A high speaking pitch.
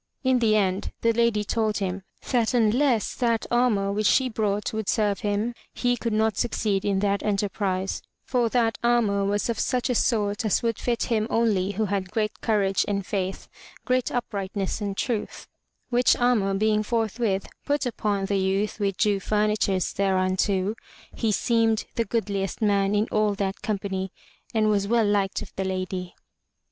Yes: high, 210 Hz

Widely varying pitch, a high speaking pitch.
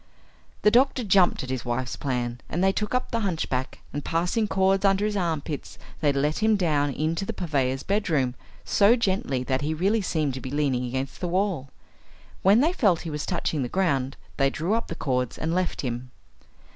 No: wide, 6.5 semitones; medium, 160 Hz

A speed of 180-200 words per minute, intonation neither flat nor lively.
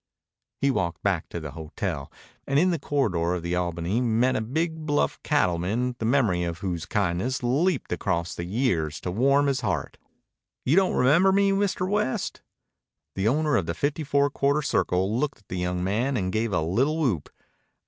No: average, 185 wpm; wide, 8.1 semitones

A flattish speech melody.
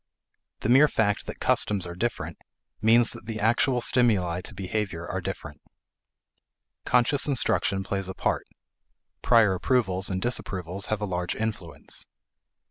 No: average, 4.1 semitones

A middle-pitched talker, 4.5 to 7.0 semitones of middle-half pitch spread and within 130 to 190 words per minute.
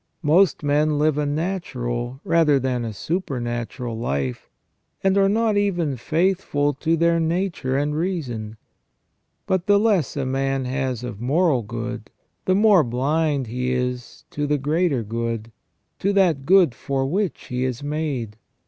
Yes: medium, 145 Hz; wide, 5.5 semitones; average, 150 wpm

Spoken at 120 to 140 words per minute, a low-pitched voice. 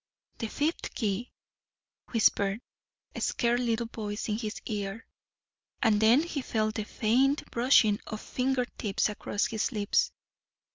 No: slow, 135 wpm; high, 225 Hz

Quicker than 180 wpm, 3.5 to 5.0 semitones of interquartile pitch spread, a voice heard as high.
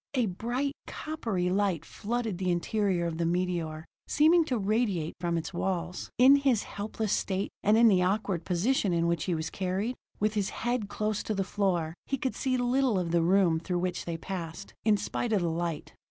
Yes: average, 195 wpm; average, 4.5 semitones; high, 195 Hz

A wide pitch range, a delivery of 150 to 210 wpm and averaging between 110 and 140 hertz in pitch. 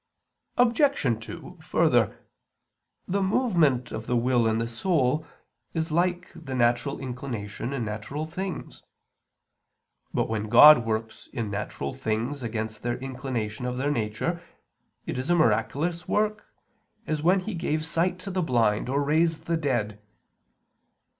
No: wide, 6.5 semitones; average, 140 wpm; low, 135 Hz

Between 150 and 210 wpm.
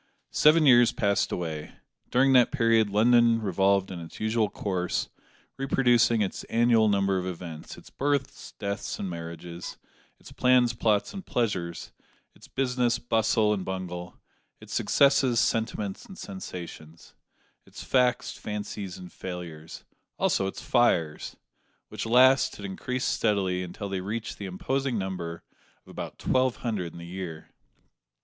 No: average, 140 wpm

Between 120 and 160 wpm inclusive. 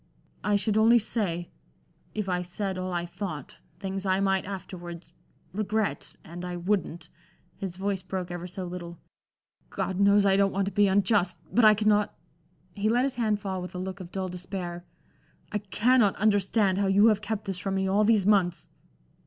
No: average, 185 wpm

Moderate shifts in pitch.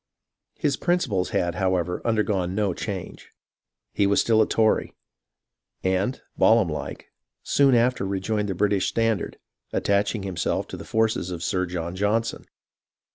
Yes: average, 3.3 semitones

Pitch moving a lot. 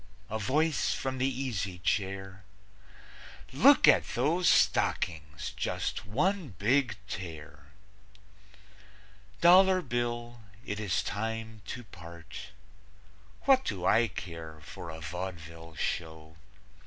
Yes: wide, 6.8 semitones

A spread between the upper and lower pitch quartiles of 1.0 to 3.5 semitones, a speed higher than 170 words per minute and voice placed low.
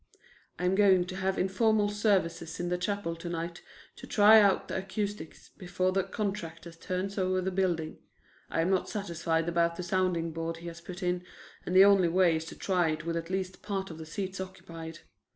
No: narrow, 2.5 semitones; average, 200 wpm; medium, 180 Hz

